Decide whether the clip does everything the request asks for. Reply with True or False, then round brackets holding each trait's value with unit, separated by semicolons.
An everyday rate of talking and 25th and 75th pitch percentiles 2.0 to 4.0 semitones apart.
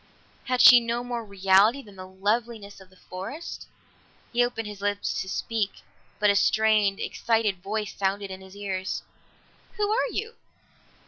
True (155 wpm; 3.3 semitones)